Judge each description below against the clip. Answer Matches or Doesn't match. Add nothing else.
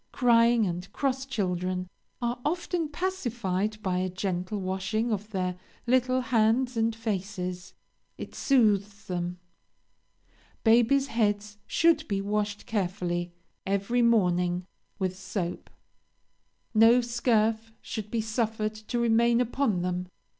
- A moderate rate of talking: Doesn't match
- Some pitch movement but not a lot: Matches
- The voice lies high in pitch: Matches